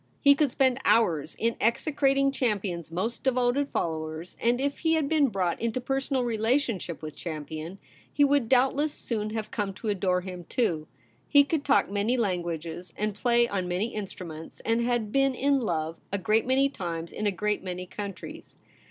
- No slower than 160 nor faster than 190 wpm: Yes, average, 180 wpm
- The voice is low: No, high, 220 Hz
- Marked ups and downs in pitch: Yes, wide, 6.5 semitones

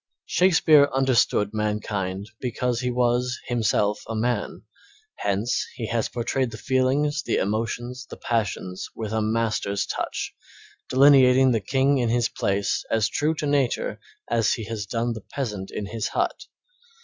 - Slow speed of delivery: No, average, 150 wpm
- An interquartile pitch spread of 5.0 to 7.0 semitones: No, average, 3.4 semitones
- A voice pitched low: Yes, low, 115 Hz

